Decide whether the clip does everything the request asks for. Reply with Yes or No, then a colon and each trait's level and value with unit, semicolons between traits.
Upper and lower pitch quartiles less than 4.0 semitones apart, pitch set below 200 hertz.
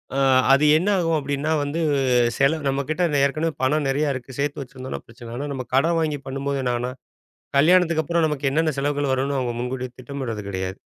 Yes: average, 2.9 semitones; medium, 140 Hz